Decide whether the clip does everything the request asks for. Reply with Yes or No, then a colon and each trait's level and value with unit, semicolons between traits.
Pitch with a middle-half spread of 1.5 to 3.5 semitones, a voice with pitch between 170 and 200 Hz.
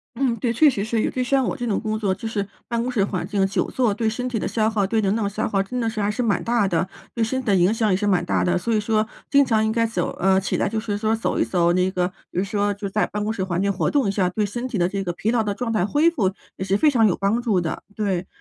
No: average, 2.9 semitones; high, 215 Hz